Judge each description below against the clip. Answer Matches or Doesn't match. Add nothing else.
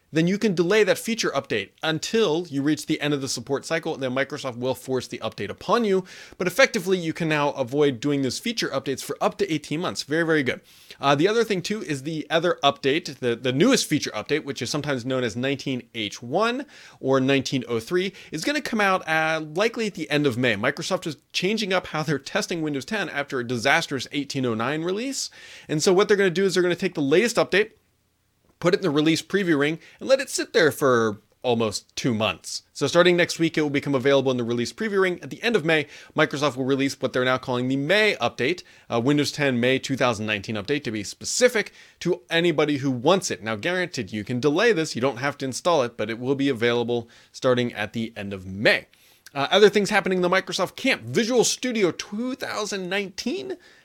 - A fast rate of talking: Matches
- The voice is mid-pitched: Matches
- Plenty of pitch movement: Matches